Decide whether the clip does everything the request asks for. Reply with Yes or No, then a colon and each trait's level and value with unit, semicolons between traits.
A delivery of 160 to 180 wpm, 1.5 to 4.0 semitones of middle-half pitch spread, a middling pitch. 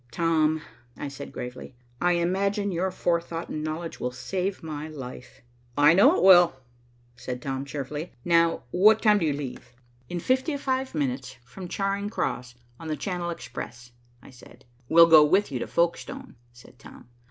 No: average, 165 wpm; average, 5.3 semitones; medium, 165 Hz